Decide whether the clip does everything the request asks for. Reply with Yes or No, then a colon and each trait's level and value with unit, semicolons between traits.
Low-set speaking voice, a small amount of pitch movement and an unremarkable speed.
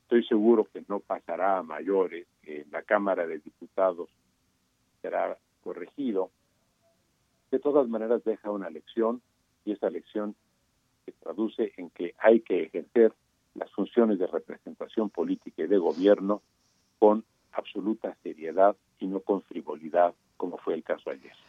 Yes: low, 110 Hz; narrow, 2.1 semitones; average, 140 wpm